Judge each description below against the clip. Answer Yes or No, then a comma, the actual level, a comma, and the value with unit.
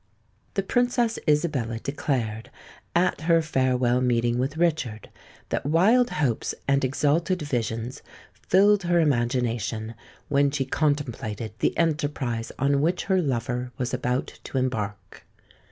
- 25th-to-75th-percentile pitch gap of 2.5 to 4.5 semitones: No, average, 5.2 semitones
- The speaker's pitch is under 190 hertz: Yes, low, 135 Hz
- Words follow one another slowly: Yes, slow, 120 wpm